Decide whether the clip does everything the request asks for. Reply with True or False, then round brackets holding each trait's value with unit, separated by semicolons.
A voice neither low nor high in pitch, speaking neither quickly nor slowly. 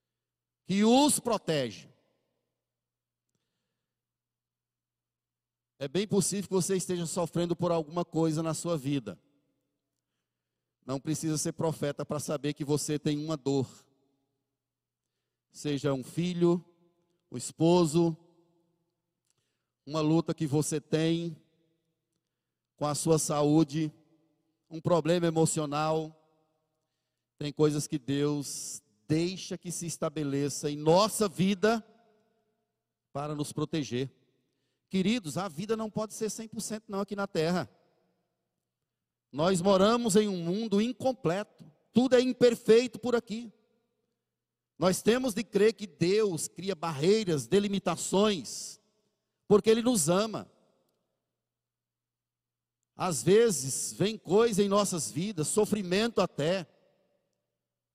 False (165 Hz; 105 wpm)